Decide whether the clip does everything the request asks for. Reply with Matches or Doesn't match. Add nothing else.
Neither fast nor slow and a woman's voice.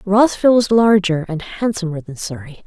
Matches